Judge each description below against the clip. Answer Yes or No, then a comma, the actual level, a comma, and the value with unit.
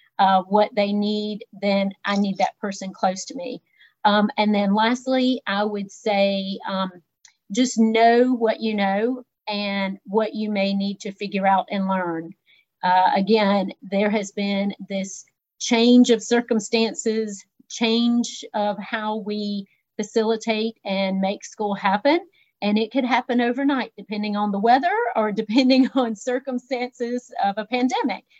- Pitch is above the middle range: Yes, high, 210 Hz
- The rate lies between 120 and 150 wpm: Yes, average, 145 wpm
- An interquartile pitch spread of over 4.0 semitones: No, average, 3.1 semitones